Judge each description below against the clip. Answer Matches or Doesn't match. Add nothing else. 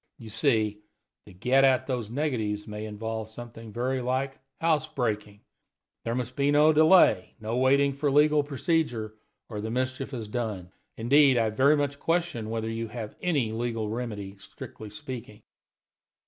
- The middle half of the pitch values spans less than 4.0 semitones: Doesn't match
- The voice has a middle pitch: Doesn't match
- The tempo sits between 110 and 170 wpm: Matches